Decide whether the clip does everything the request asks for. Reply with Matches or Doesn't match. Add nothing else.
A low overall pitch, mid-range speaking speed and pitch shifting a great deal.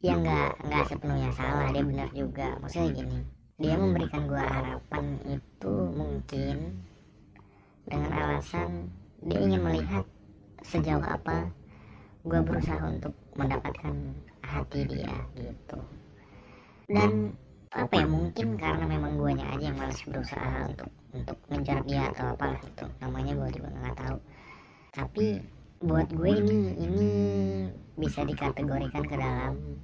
Doesn't match